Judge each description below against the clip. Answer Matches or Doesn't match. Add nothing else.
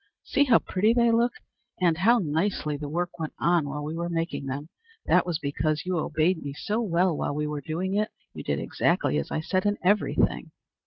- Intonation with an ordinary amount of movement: Matches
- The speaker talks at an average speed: Doesn't match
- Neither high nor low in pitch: Matches